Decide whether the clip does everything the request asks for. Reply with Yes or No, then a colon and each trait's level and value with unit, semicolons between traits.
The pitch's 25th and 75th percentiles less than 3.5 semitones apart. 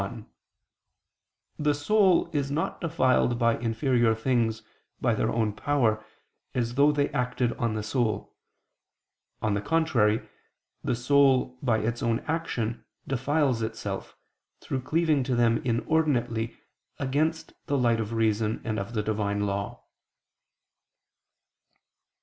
No: average, 4.1 semitones